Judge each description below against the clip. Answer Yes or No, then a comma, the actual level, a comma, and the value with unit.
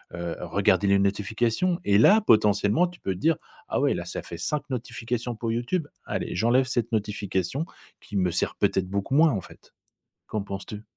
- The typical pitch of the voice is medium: No, low, 110 Hz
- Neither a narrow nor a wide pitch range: Yes, average, 4.2 semitones